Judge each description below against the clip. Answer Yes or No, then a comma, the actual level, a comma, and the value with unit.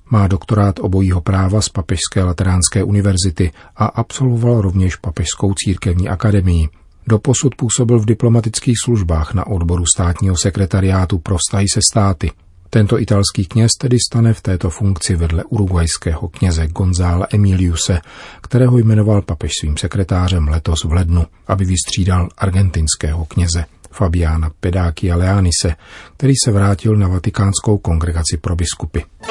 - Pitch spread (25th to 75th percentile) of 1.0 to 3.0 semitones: No, average, 3.4 semitones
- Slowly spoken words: No, average, 125 wpm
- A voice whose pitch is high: No, very low, 95 Hz